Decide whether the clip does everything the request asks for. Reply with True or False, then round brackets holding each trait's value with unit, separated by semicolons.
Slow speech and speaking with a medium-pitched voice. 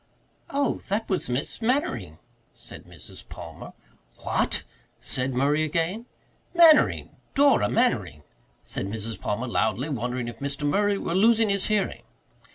True (130 wpm; 155 Hz)